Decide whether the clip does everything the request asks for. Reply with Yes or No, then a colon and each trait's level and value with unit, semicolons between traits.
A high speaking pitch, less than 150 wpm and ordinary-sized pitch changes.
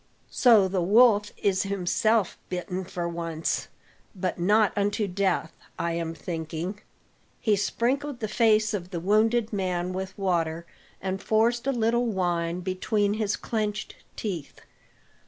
Yes: high, 195 Hz; slow, 135 wpm; average, 3.5 semitones